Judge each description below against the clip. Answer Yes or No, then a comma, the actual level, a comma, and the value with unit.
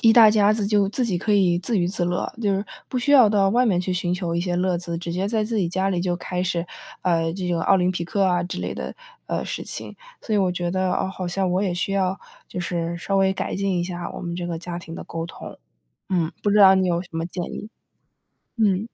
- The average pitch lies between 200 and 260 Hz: No, medium, 185 Hz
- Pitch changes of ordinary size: No, narrow, 2.2 semitones